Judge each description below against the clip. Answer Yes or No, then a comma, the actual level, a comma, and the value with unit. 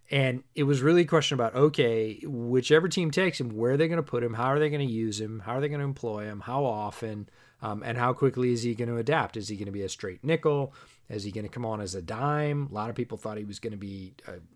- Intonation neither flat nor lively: Yes, average, 4.7 semitones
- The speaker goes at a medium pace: No, fast, 295 wpm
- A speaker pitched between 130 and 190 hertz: No, low, 120 Hz